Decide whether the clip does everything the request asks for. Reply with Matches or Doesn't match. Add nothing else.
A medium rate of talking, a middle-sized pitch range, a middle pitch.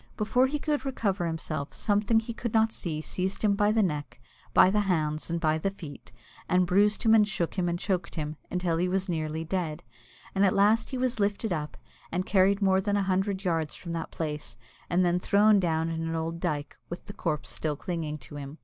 Doesn't match